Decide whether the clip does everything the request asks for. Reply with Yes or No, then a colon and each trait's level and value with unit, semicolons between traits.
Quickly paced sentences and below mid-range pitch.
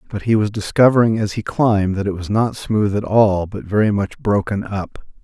Yes: fast, 220 wpm; low, 105 Hz